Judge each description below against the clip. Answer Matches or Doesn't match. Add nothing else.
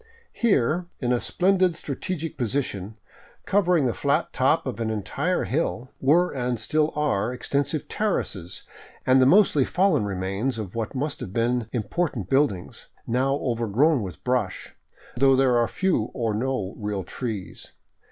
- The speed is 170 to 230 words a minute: Doesn't match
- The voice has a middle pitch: Doesn't match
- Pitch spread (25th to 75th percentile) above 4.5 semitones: Matches